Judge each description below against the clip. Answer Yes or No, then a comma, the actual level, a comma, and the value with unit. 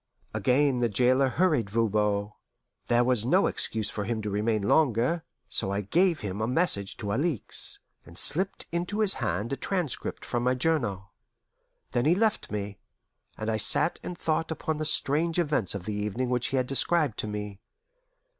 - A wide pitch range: Yes, wide, 7.0 semitones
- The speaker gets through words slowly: No, average, 175 wpm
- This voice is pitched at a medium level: No, low, 125 Hz